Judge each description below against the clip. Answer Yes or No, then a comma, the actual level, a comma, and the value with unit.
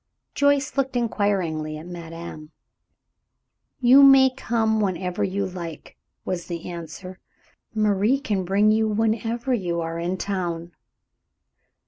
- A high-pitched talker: Yes, high, 195 Hz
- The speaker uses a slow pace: Yes, slow, 115 wpm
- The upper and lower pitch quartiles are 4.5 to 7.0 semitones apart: Yes, average, 4.8 semitones